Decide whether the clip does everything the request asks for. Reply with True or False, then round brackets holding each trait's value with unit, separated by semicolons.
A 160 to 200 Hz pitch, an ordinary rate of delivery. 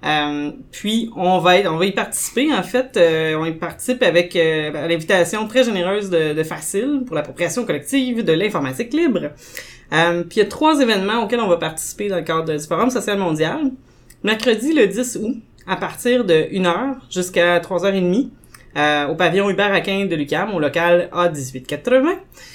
True (185 Hz; 175 wpm)